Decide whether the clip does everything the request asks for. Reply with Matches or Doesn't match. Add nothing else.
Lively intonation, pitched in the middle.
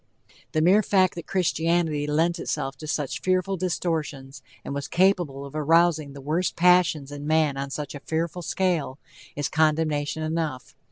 Doesn't match